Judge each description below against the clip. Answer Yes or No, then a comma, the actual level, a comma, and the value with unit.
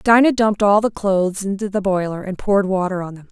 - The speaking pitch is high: Yes, high, 195 Hz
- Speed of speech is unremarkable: No, fast, 235 wpm